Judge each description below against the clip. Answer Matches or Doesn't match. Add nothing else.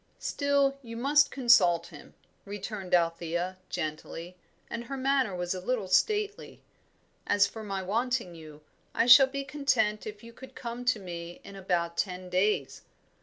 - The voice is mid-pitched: Doesn't match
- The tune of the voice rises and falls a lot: Matches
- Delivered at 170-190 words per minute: Doesn't match